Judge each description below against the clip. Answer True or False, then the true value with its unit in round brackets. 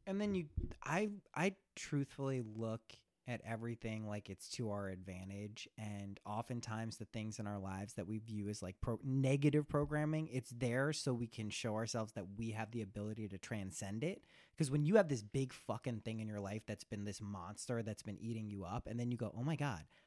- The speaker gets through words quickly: True (210 wpm)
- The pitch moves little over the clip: False (4.2 semitones)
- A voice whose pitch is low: True (115 Hz)